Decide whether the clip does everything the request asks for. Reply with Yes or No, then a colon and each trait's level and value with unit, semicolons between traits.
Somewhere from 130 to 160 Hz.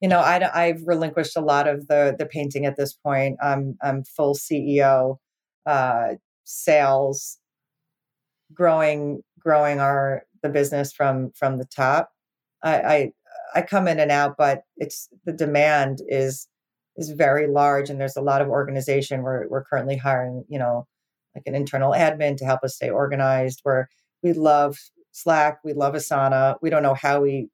Yes: medium, 140 Hz